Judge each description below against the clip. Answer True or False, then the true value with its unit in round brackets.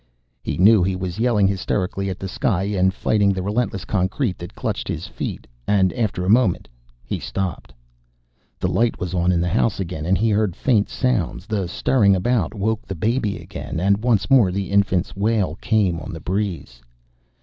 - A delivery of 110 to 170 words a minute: False (185 wpm)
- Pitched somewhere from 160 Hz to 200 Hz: False (100 Hz)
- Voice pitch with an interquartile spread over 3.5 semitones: False (2.9 semitones)